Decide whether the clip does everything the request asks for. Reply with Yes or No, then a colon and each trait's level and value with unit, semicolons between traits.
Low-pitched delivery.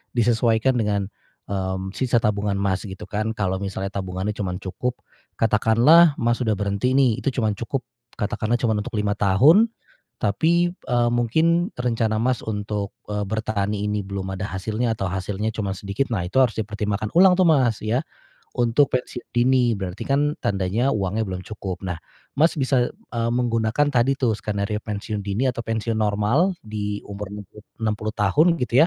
Yes: low, 110 Hz